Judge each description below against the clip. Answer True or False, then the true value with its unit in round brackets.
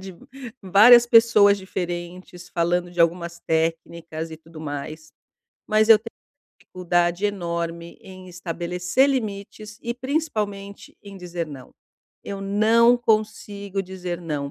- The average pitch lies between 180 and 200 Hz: True (185 Hz)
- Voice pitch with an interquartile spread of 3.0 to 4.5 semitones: True (3.7 semitones)